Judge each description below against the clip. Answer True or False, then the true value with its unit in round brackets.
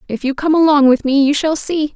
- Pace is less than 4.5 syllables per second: False (5.7 syllables/s)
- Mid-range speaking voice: False (290 Hz)